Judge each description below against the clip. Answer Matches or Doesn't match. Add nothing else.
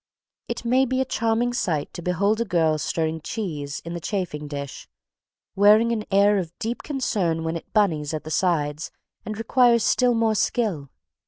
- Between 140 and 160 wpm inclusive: Doesn't match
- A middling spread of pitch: Doesn't match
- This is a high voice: Matches